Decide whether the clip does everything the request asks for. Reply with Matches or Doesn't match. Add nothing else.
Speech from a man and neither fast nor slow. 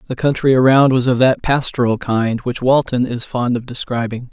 Matches